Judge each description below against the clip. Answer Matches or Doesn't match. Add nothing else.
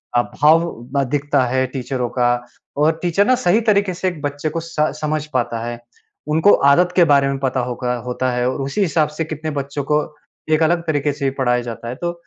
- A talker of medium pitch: Matches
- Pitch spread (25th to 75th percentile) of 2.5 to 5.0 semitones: Matches